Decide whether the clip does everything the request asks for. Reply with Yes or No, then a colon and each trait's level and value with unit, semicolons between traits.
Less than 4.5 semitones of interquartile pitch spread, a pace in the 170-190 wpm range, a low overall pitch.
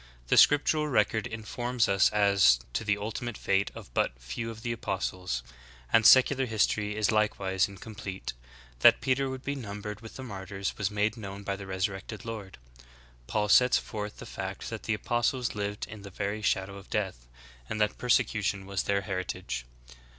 Yes: narrow, 2.6 semitones; average, 180 wpm; low, 105 Hz